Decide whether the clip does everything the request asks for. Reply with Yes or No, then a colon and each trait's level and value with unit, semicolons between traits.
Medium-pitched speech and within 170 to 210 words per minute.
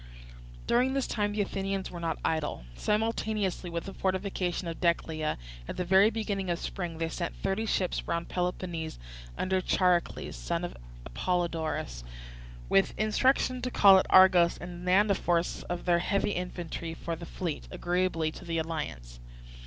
No: medium, 180 Hz; average, 160 wpm